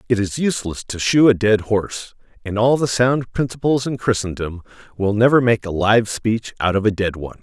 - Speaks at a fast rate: Yes, fast, 210 wpm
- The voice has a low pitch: Yes, low, 110 Hz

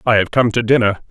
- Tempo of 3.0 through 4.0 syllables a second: No, 6.5 syllables/s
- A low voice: Yes, low, 115 Hz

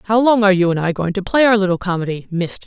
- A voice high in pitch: Yes, high, 195 Hz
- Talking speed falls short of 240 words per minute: No, fast, 295 wpm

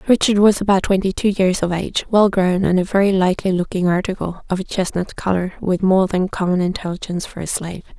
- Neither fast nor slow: No, fast, 210 wpm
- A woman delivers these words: Yes, female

